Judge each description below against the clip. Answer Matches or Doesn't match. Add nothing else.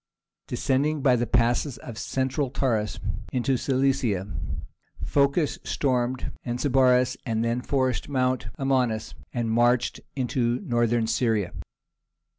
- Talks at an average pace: Doesn't match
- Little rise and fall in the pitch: Matches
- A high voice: Doesn't match